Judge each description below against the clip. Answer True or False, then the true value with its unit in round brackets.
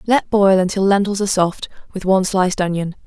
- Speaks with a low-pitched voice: False (190 Hz)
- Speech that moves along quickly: False (195 wpm)